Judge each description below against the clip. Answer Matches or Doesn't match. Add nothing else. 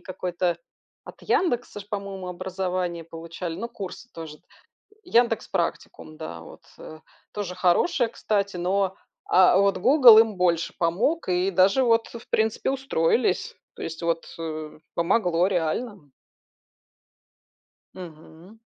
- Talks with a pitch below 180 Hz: Doesn't match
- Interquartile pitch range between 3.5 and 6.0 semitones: Matches